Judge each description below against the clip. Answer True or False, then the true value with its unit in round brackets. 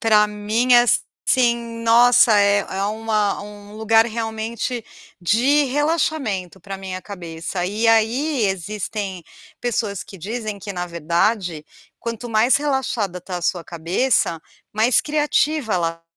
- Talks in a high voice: True (215 Hz)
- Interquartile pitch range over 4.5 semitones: False (3.6 semitones)